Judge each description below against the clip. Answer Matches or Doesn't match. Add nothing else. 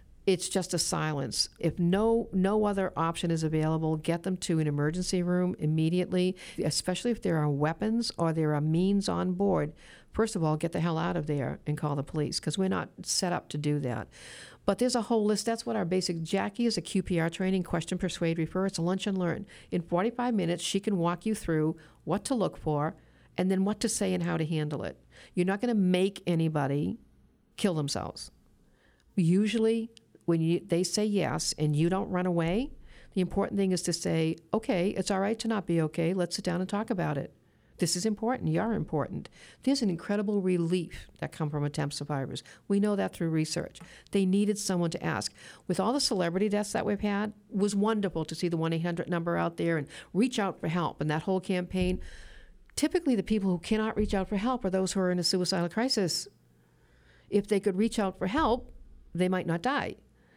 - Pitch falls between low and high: Matches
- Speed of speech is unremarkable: Doesn't match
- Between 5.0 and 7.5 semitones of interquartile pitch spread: Doesn't match